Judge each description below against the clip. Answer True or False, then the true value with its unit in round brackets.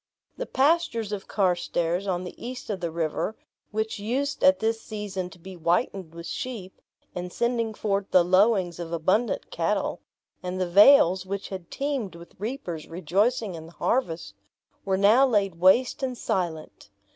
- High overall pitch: True (195 Hz)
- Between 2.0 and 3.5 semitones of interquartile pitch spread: False (4.5 semitones)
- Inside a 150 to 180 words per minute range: True (160 wpm)